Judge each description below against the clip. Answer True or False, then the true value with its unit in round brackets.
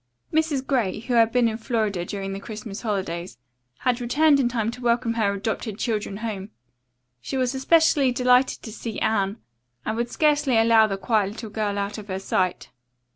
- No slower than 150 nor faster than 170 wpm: False (180 wpm)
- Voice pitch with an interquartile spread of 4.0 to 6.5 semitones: False (3.5 semitones)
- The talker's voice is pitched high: True (225 Hz)